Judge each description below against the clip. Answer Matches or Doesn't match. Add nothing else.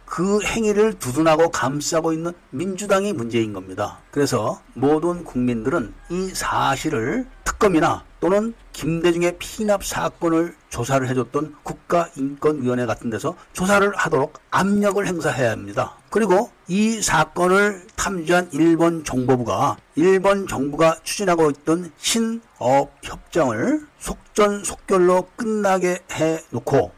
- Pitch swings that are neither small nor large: Doesn't match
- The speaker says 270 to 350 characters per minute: Matches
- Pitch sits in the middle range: Matches